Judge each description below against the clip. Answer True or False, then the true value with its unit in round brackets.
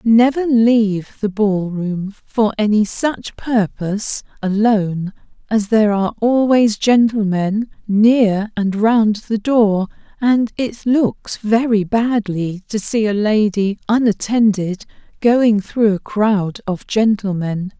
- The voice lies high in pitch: True (215 Hz)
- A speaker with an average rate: False (120 wpm)